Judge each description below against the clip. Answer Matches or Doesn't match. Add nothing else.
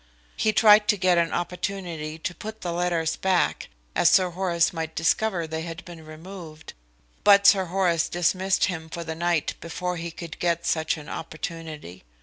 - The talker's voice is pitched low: Doesn't match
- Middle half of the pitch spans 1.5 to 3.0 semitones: Matches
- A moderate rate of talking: Matches